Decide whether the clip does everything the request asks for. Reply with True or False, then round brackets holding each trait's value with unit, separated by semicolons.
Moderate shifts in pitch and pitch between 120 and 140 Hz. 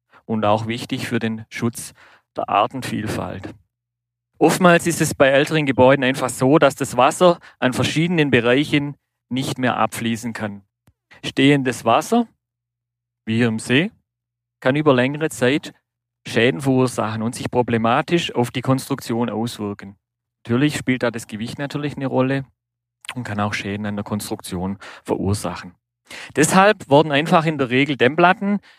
True (3.5 semitones; 125 Hz)